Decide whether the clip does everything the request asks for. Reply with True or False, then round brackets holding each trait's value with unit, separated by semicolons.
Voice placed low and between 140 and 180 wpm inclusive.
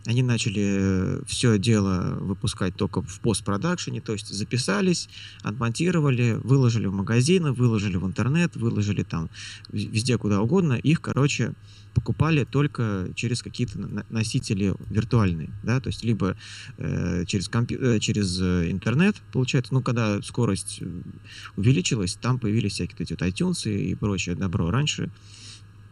False (110 Hz; 130 wpm)